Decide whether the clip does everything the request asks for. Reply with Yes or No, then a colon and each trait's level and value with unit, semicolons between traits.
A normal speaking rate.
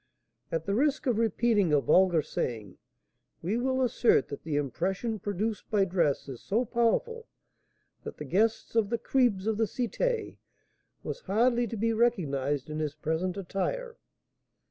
Yes: average, 155 wpm